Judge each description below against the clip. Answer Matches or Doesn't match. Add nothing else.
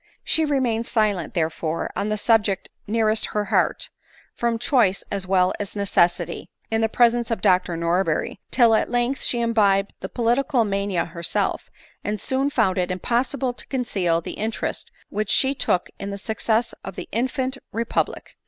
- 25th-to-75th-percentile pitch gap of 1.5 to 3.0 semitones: Doesn't match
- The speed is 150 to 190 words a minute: Matches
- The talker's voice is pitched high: Matches